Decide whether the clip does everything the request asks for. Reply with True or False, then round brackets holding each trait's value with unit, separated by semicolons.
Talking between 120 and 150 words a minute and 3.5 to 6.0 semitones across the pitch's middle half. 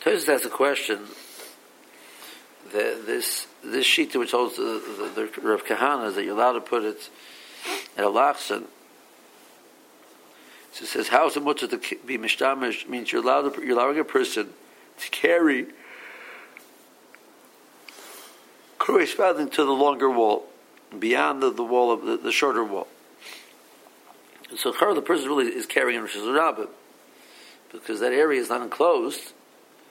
True (140 wpm; 3.9 semitones)